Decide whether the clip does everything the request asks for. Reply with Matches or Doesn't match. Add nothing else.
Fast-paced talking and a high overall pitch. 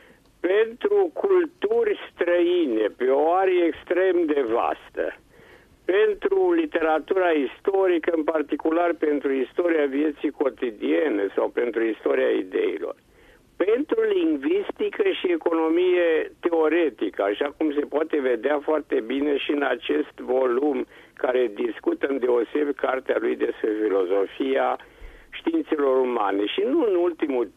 Doesn't match